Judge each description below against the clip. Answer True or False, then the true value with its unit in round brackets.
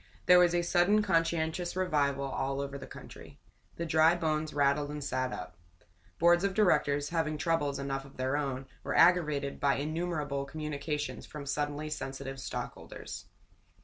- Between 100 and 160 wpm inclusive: True (150 wpm)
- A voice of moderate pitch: True (150 Hz)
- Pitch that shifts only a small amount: False (3.1 semitones)